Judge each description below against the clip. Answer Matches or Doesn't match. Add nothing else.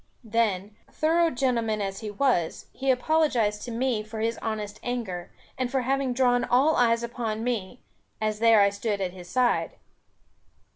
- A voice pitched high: Matches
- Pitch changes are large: Doesn't match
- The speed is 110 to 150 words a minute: Doesn't match